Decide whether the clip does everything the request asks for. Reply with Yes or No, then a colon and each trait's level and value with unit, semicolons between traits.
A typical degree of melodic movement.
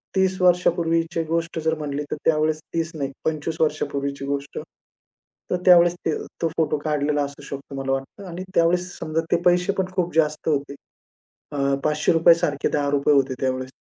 Yes: average, 3.0 semitones